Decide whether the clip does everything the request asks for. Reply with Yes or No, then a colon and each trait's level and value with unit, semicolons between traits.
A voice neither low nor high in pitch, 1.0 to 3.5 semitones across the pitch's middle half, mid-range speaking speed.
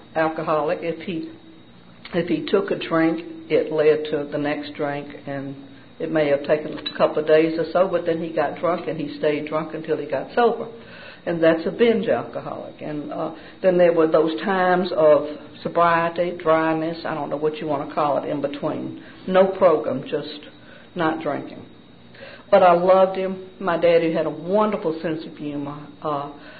Yes: medium, 160 Hz; narrow, 2.5 semitones; average, 185 wpm